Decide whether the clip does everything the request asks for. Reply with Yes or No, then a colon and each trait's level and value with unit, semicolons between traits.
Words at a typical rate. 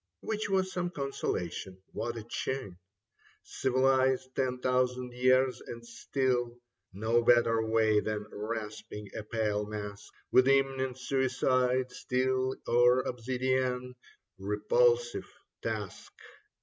No: slow, 105 wpm